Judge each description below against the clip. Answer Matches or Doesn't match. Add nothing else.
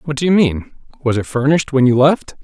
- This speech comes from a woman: Doesn't match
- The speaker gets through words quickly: Matches